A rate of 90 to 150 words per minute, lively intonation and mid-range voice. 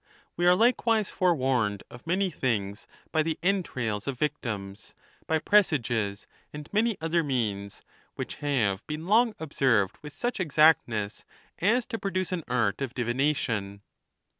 Yes: average, 145 wpm; wide, 8.1 semitones; medium, 145 Hz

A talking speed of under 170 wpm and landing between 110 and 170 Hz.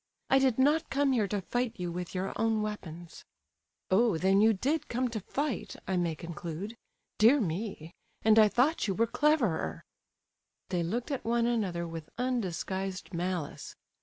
No: average, 160 wpm; high, 210 Hz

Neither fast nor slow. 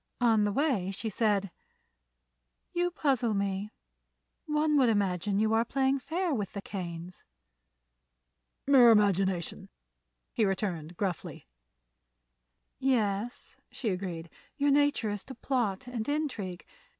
No: slow, 115 wpm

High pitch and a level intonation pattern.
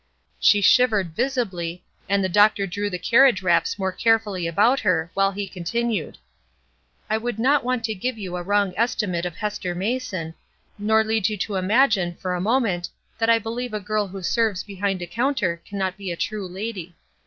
No: high, 205 Hz; average, 3.6 semitones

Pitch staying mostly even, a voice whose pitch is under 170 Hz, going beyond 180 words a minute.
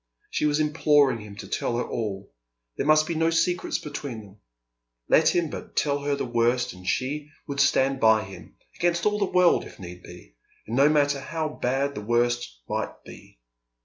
No: average, 5.1 semitones; medium, 140 Hz; average, 190 wpm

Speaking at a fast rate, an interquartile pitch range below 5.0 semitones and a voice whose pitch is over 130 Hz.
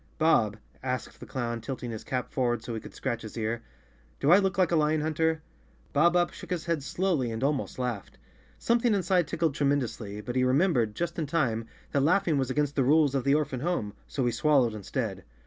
No: fast, 215 wpm; average, 5.3 semitones; medium, 140 Hz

